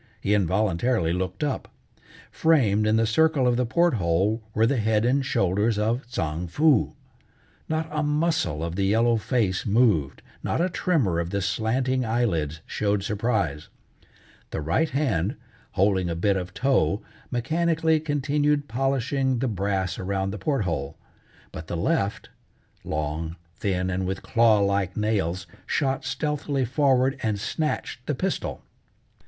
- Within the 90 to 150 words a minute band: Yes, average, 145 wpm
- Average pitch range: No, wide, 6.1 semitones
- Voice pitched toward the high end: No, low, 110 Hz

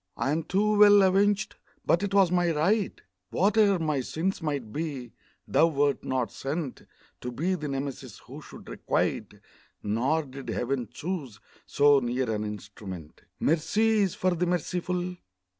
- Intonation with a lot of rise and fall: Yes, wide, 6.0 semitones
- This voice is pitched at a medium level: Yes, medium, 155 Hz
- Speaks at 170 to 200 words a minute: No, average, 145 wpm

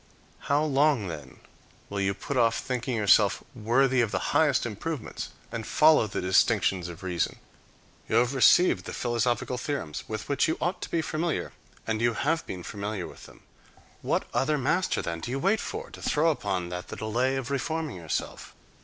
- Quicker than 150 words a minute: Yes, average, 180 wpm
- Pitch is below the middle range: Yes, low, 120 Hz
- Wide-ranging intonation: Yes, wide, 6.1 semitones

